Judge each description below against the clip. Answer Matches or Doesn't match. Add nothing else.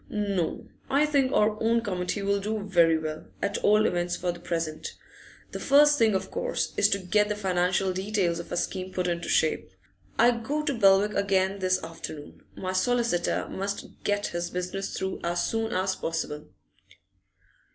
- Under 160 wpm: Doesn't match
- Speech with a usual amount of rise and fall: Matches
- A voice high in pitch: Matches